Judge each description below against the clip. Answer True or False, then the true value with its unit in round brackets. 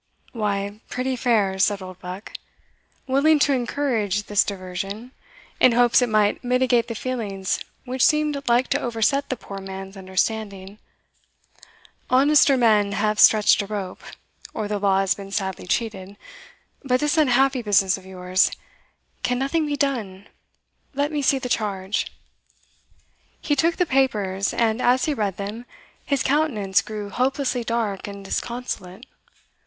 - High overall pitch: True (220 Hz)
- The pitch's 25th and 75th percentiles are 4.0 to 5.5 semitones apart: True (4.7 semitones)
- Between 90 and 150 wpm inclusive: True (140 wpm)